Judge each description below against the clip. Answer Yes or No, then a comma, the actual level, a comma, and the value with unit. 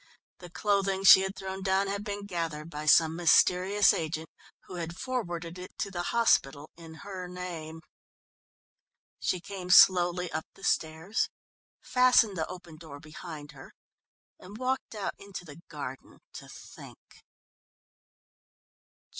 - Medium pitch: Yes, medium, 180 Hz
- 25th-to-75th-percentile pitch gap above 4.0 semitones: No, average, 3.4 semitones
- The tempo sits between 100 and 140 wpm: Yes, slow, 135 wpm